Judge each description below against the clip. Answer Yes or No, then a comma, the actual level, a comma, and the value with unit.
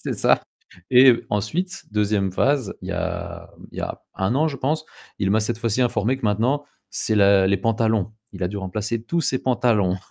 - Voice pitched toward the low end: Yes, low, 110 Hz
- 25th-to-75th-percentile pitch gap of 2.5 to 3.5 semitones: No, average, 4.4 semitones